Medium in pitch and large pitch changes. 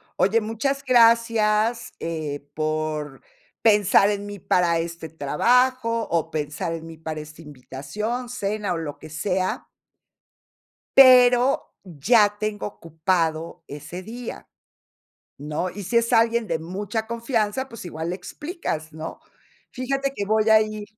No: high, 205 Hz; wide, 6.2 semitones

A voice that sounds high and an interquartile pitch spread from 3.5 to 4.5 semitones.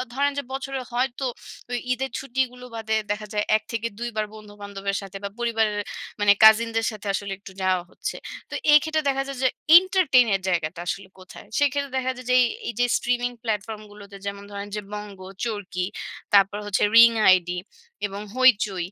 Yes: high, 220 Hz; average, 3.9 semitones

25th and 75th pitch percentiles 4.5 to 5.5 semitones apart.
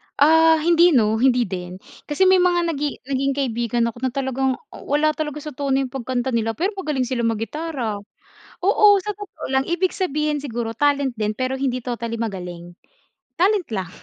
Yes: average, 5.0 semitones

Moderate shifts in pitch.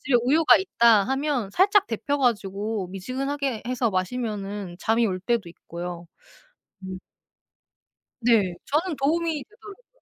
No: wide, 6.7 semitones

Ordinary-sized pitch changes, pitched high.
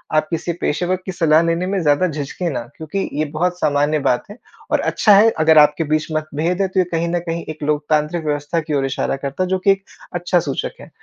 No: average, 3.1 semitones; medium, 160 Hz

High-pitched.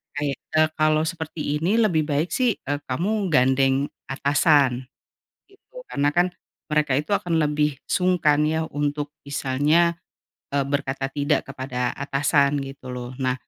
No: medium, 145 Hz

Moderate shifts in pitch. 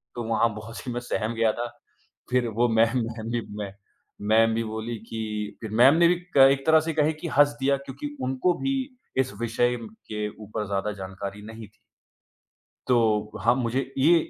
Yes: average, 3.3 semitones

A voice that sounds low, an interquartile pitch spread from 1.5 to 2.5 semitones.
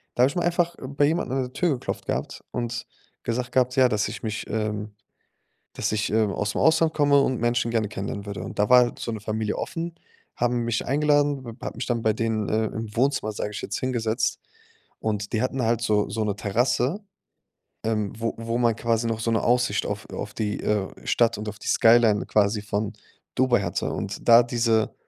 No: low, 115 Hz; average, 2.9 semitones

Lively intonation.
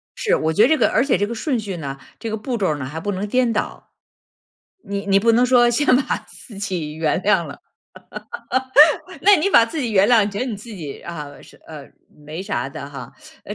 Yes: wide, 6.8 semitones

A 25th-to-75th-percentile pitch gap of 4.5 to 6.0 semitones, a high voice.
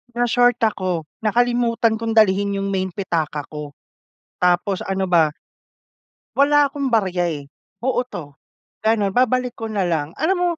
Yes: average, 5.3 semitones; high, 205 Hz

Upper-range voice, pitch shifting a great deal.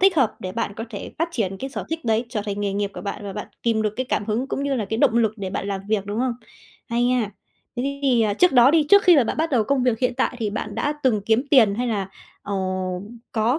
No: high, 230 Hz; average, 4.2 semitones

